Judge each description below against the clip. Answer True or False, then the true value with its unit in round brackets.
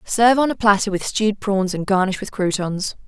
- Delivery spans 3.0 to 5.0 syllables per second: False (5.5 syllables/s)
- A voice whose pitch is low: False (205 Hz)